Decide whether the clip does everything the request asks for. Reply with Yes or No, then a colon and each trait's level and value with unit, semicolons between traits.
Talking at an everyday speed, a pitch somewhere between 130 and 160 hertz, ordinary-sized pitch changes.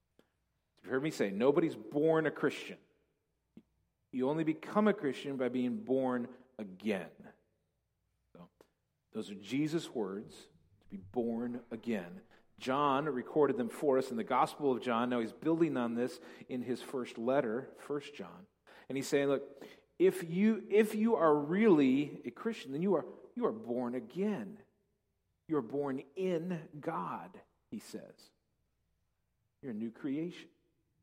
No: average, 145 wpm; medium, 140 Hz; wide, 5.8 semitones